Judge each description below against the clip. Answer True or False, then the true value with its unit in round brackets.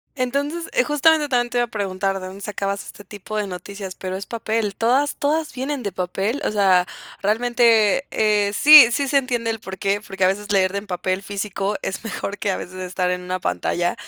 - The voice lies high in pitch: True (205 Hz)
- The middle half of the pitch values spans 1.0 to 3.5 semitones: False (4.2 semitones)